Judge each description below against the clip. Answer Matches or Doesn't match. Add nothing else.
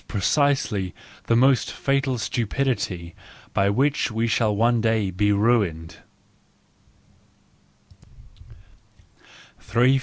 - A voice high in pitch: Doesn't match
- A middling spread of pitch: Matches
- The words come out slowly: Matches